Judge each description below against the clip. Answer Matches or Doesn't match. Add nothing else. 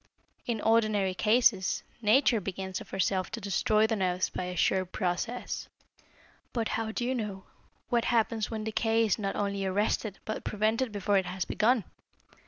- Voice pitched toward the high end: Matches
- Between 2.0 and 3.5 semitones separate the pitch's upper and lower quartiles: Matches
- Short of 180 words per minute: Matches